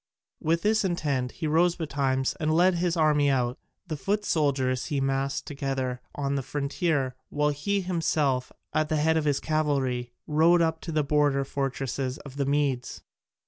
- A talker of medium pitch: Yes, medium, 145 Hz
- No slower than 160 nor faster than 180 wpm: Yes, average, 170 wpm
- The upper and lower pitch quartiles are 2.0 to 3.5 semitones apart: Yes, average, 3.0 semitones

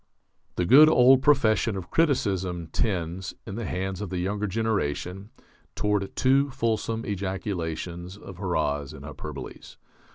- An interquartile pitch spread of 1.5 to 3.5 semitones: No, average, 4.2 semitones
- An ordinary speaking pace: No, slow, 130 wpm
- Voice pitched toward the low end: Yes, very low, 95 Hz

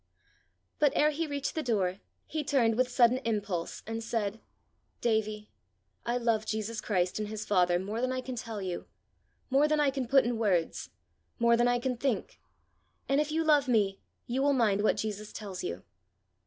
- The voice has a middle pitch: No, high, 230 Hz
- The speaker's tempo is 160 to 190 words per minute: Yes, average, 185 wpm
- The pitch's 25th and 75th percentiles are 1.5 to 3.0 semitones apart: No, average, 4.1 semitones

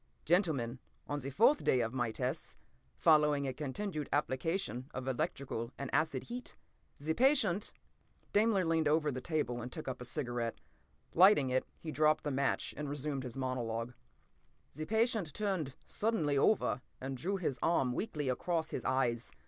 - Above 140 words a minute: Yes, average, 160 wpm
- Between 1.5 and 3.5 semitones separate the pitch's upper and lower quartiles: No, average, 4.7 semitones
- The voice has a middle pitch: Yes, medium, 145 Hz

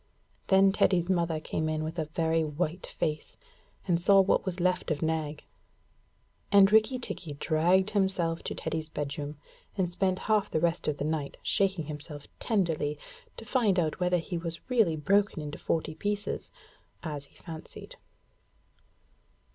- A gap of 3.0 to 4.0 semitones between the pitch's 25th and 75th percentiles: Yes, average, 3.6 semitones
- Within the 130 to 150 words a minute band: Yes, average, 145 wpm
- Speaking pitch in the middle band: Yes, medium, 170 Hz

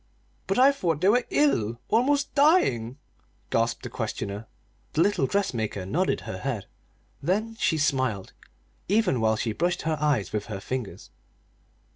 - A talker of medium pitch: Yes, medium, 145 Hz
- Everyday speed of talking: Yes, average, 145 wpm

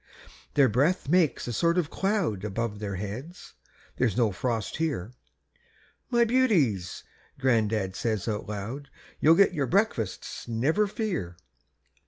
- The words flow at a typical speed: No, slow, 130 wpm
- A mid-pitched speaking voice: No, low, 125 Hz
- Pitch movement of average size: No, wide, 8.3 semitones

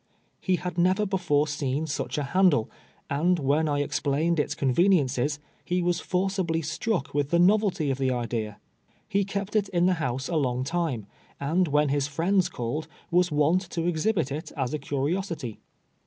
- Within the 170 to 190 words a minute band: Yes, average, 175 wpm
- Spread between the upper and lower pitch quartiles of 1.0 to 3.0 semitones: No, average, 4.3 semitones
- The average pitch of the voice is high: No, medium, 155 Hz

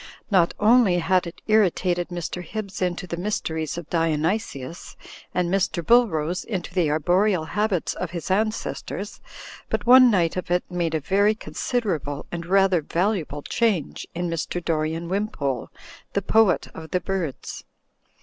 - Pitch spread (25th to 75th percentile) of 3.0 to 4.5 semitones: Yes, average, 3.4 semitones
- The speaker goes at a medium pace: Yes, average, 150 wpm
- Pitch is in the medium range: Yes, medium, 180 Hz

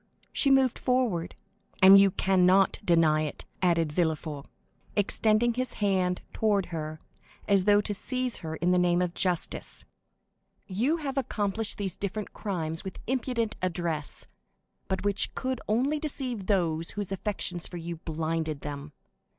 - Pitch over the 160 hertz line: Yes, high, 190 Hz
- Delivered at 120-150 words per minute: Yes, average, 140 wpm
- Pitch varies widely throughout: No, average, 4.6 semitones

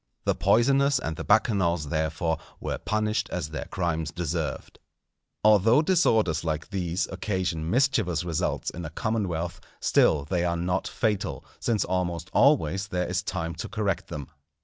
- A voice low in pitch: Yes, very low, 90 Hz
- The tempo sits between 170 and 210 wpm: No, average, 150 wpm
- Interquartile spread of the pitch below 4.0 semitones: No, average, 4.6 semitones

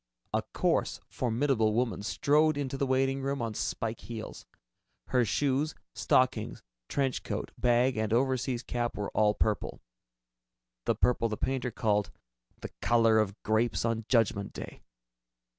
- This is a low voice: Yes, low, 120 Hz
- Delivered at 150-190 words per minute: No, average, 140 wpm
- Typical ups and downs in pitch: Yes, average, 3.3 semitones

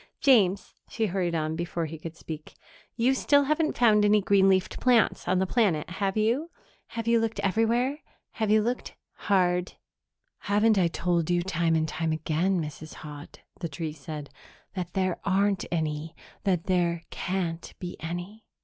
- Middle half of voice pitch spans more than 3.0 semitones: Yes, average, 4.6 semitones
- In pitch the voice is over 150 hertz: Yes, medium, 185 Hz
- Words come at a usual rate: Yes, average, 165 wpm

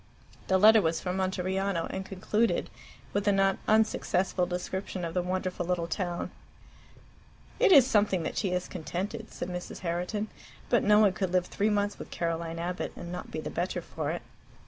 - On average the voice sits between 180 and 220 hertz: Yes, medium, 185 Hz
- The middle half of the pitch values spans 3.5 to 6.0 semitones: No, narrow, 2.5 semitones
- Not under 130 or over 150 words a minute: No, average, 180 wpm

